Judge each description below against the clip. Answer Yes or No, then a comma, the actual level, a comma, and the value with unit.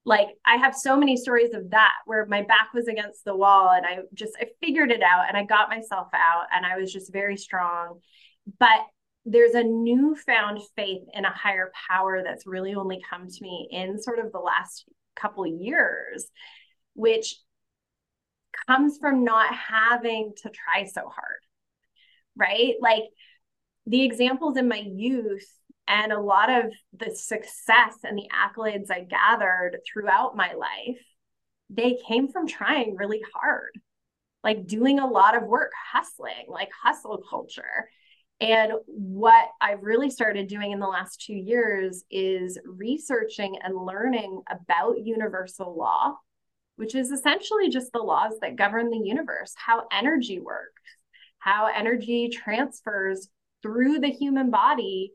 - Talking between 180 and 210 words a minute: No, average, 150 wpm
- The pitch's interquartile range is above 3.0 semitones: Yes, average, 3.8 semitones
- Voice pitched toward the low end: No, high, 220 Hz